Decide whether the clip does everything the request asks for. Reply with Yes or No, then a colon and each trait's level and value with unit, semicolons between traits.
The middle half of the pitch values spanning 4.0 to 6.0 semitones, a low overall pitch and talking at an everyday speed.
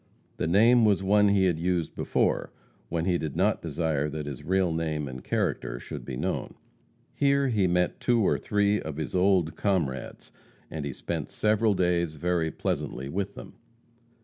Yes: average, 4.4 semitones; very low, 90 Hz; average, 175 wpm